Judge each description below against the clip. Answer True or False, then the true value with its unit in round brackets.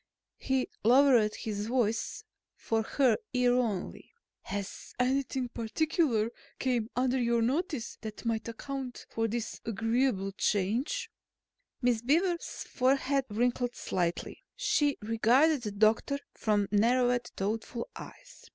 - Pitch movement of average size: True (3.3 semitones)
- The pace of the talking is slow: True (115 wpm)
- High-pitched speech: True (240 Hz)